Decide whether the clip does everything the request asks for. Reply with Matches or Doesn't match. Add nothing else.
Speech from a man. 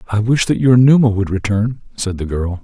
Matches